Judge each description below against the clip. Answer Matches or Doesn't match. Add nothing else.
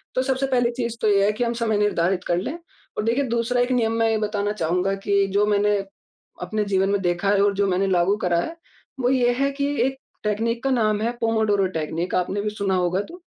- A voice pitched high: Matches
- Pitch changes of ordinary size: Matches